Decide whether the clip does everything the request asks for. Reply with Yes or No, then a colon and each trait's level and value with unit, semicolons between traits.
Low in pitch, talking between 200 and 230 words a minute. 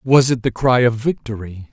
Yes: low, 120 Hz; fast, 210 wpm